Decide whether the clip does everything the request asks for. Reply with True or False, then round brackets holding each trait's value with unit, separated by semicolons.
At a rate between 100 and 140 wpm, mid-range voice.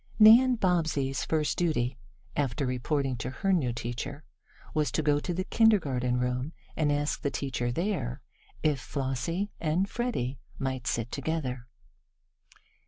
True (135 wpm; 145 Hz)